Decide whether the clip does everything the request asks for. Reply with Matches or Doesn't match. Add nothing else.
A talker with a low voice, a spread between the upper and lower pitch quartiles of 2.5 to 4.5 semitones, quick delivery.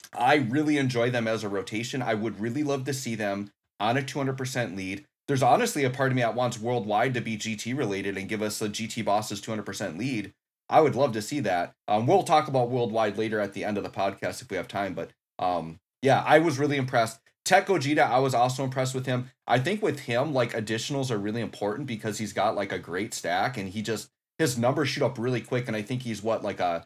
Matches